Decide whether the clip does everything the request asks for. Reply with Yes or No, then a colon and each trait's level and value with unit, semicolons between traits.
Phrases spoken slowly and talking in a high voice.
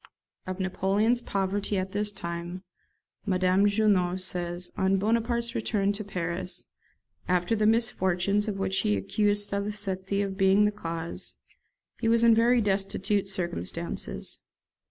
Yes: slow, 130 wpm; high, 195 Hz